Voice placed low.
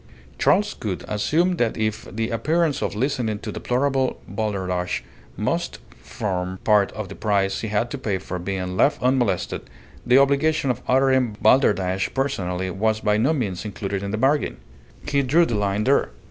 Yes: low, 110 Hz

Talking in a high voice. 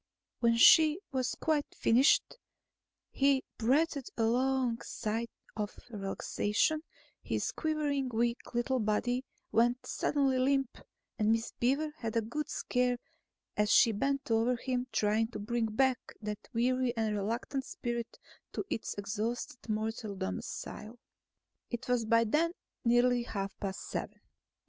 Yes: high, 240 Hz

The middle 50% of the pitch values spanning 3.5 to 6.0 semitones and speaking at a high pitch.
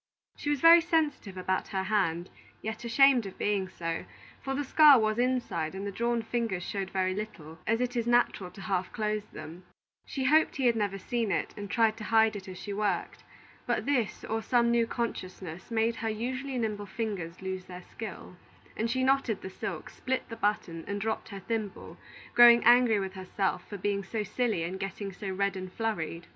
Yes: average, 3.9 semitones; high, 215 Hz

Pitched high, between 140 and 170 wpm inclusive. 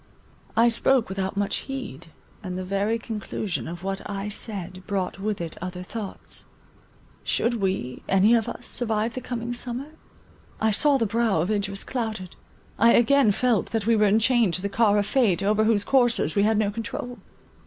No: high, 210 Hz; average, 180 wpm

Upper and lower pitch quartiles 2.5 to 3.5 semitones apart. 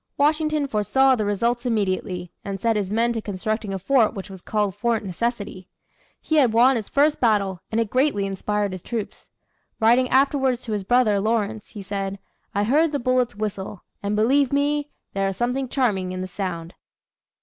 No: average, 4.3 semitones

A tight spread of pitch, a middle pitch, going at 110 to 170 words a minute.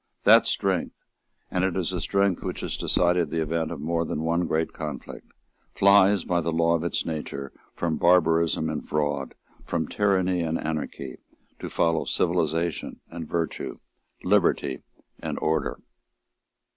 No: narrow, 2.1 semitones; very low, 85 Hz; average, 145 wpm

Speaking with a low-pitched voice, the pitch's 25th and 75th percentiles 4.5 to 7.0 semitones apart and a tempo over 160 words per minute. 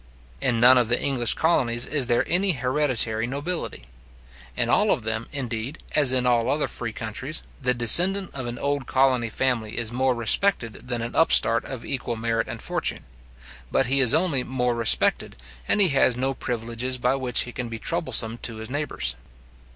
No: low, 125 Hz; average, 2.8 semitones; average, 180 wpm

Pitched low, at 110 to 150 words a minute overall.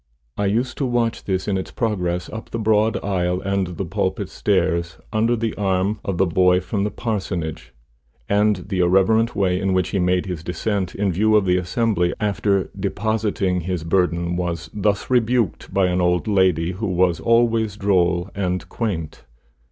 No: very low, 95 Hz; average, 175 wpm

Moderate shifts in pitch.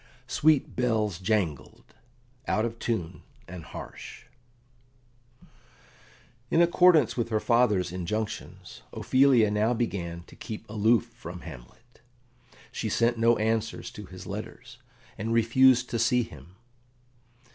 Yes: average, 3.0 semitones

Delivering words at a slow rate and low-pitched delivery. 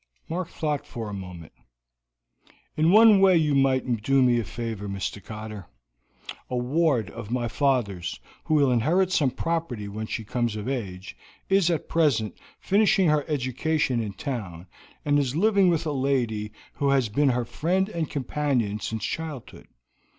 No: average, 160 wpm; low, 130 Hz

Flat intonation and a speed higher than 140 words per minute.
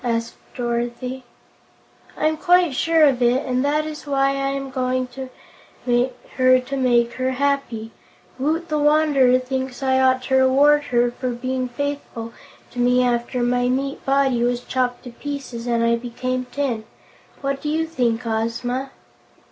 Yes: narrow, 2.2 semitones; average, 155 wpm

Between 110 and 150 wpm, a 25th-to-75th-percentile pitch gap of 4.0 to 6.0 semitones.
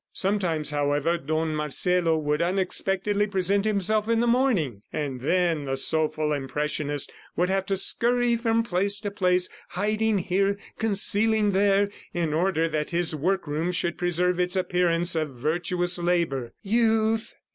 Yes: average, 140 wpm; average, 4.4 semitones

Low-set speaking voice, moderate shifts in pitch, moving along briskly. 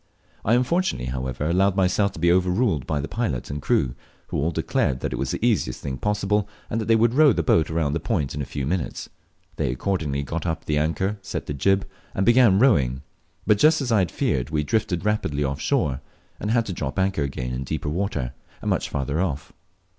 No: very low, 85 Hz; wide, 6.6 semitones; fast, 220 wpm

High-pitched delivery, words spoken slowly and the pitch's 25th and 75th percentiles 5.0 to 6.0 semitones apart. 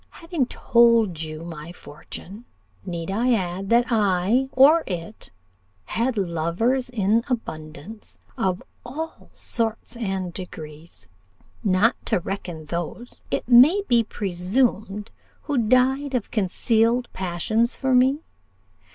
Yes: high, 215 Hz; slow, 115 wpm; wide, 5.6 semitones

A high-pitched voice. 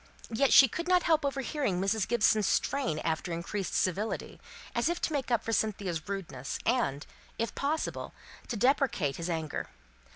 Yes: high, 220 Hz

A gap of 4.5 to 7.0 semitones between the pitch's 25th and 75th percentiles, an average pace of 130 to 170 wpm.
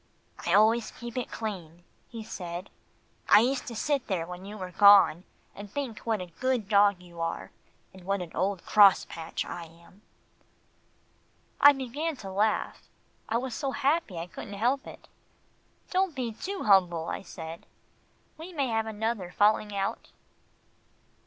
Yes: average, 5.0 semitones; average, 155 wpm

